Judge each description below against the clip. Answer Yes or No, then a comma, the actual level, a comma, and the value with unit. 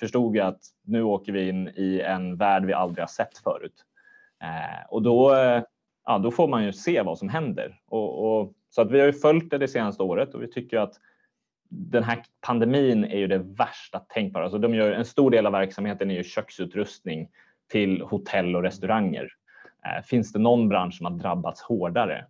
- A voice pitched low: Yes, low, 110 Hz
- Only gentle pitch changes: No, average, 4.2 semitones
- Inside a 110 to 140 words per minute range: No, fast, 195 wpm